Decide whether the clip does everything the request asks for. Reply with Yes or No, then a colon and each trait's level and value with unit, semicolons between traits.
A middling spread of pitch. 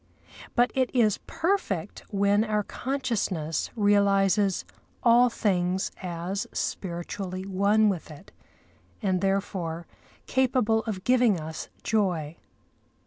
Yes: average, 3.5 semitones